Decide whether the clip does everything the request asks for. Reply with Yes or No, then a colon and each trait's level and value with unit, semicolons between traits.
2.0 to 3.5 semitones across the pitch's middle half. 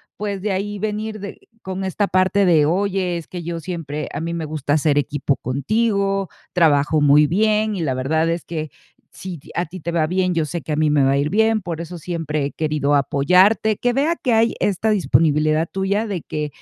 No: average, 4.6 semitones